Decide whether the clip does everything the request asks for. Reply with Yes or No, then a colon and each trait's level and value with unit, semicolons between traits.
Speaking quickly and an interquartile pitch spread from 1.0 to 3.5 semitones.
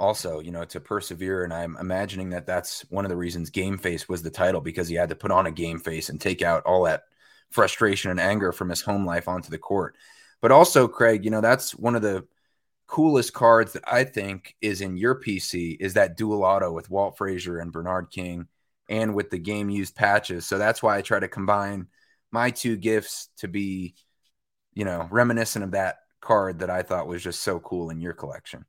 Yes: fast, 220 wpm; average, 3.0 semitones